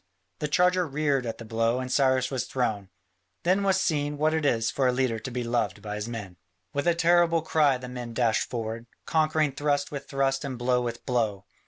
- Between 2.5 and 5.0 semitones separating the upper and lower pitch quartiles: Yes, average, 4.3 semitones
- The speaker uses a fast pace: Yes, fast, 210 wpm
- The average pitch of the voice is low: Yes, low, 130 Hz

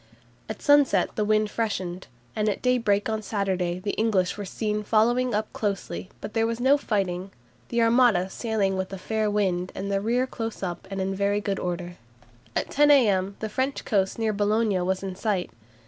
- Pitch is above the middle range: Yes, high, 210 Hz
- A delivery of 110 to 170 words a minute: No, average, 190 wpm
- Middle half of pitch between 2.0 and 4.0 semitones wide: Yes, average, 2.9 semitones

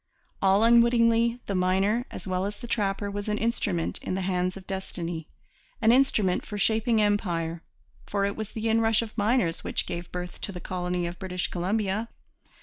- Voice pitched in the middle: No, high, 200 Hz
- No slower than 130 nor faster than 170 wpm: No, average, 180 wpm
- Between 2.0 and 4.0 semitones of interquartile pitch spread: Yes, average, 3.6 semitones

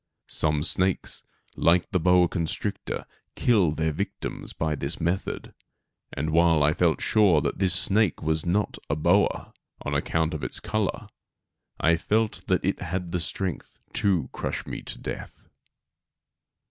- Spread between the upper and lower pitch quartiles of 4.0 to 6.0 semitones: No, average, 3.2 semitones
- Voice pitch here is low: Yes, very low, 85 Hz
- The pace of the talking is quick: No, average, 145 wpm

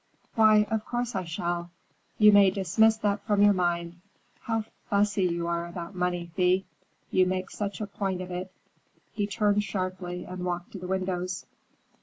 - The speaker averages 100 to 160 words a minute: No, average, 170 wpm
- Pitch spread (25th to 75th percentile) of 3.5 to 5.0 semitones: No, narrow, 2.5 semitones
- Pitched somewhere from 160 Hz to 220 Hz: Yes, medium, 185 Hz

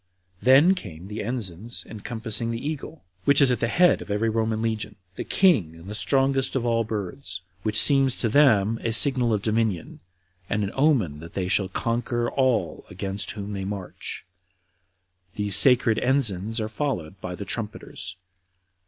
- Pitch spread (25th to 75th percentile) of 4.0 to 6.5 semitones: Yes, average, 4.3 semitones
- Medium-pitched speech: No, low, 110 Hz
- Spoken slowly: No, average, 165 wpm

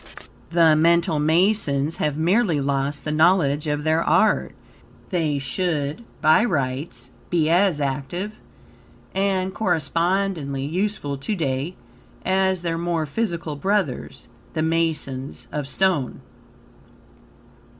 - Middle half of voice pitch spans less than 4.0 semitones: No, average, 4.3 semitones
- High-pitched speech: No, medium, 160 Hz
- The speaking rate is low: Yes, slow, 110 wpm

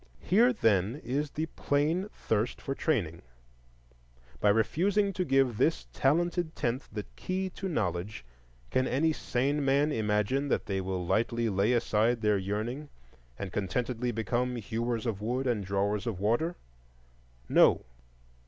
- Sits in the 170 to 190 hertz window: No, low, 120 Hz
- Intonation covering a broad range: Yes, wide, 5.7 semitones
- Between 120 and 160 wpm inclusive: Yes, average, 140 wpm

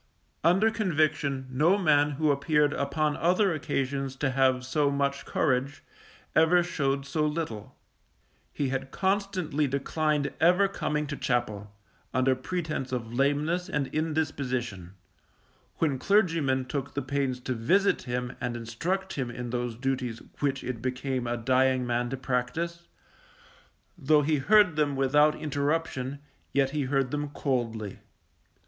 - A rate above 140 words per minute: No, slow, 135 wpm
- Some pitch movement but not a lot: Yes, average, 3.4 semitones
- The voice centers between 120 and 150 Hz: Yes, medium, 140 Hz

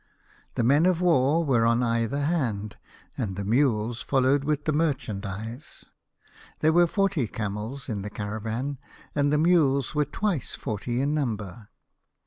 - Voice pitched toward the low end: Yes, low, 130 Hz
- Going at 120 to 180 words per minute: Yes, average, 145 wpm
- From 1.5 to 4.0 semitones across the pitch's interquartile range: No, average, 5.2 semitones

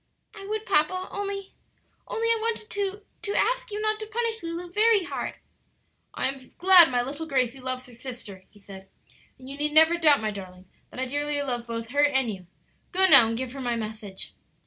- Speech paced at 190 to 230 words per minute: Yes, fast, 205 wpm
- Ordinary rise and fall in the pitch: No, wide, 8.5 semitones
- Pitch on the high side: Yes, very high, 290 Hz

